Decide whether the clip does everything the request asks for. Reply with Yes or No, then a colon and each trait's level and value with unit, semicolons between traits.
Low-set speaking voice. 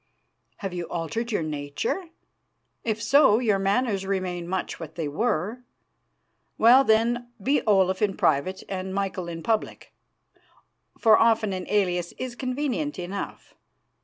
No: high, 200 Hz